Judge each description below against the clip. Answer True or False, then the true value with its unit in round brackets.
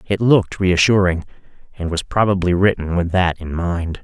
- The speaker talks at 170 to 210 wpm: False (150 wpm)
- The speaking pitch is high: False (90 Hz)